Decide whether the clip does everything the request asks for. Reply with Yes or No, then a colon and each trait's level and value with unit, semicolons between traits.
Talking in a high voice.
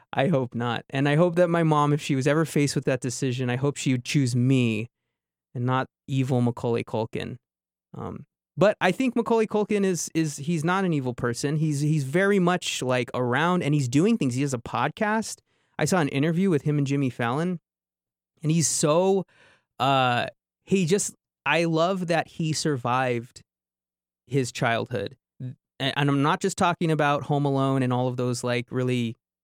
No: medium, 140 Hz